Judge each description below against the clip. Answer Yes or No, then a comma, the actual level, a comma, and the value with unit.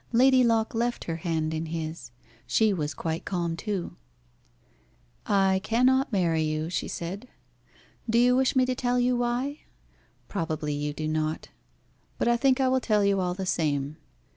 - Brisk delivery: No, average, 165 wpm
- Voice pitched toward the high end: Yes, high, 195 Hz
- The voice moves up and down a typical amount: No, wide, 7.2 semitones